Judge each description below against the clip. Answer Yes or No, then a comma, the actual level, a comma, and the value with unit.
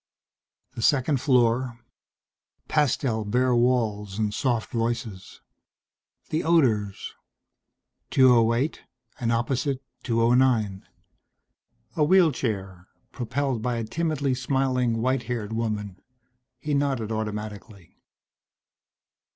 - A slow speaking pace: Yes, slow, 85 wpm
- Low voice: Yes, low, 120 Hz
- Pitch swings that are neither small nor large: Yes, average, 3.2 semitones